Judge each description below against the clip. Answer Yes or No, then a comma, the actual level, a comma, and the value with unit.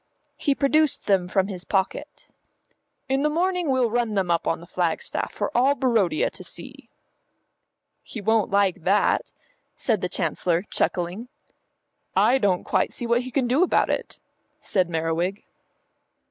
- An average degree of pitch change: No, wide, 6.1 semitones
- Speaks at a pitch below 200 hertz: No, high, 210 Hz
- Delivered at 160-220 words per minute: No, average, 150 wpm